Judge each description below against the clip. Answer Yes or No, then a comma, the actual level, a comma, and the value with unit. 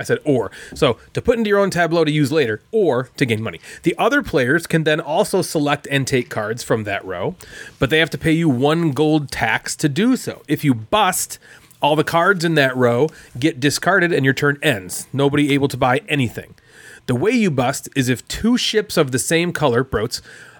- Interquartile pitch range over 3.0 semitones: Yes, average, 3.7 semitones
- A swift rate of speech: Yes, fast, 220 wpm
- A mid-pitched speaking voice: Yes, medium, 150 Hz